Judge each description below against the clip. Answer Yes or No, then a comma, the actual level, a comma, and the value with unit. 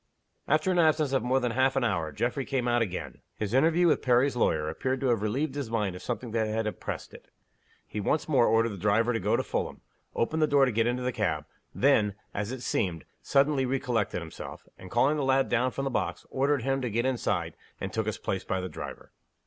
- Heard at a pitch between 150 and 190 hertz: No, low, 120 Hz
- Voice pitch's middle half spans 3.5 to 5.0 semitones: Yes, average, 4.0 semitones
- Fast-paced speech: Yes, fast, 230 wpm